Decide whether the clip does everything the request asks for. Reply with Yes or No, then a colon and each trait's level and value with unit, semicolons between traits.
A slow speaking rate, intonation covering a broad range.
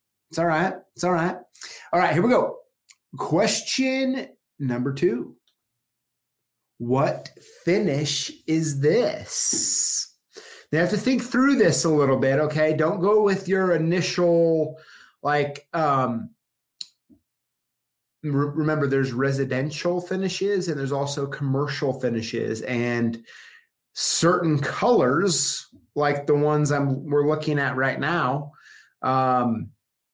No: slow, 115 wpm; average, 4.6 semitones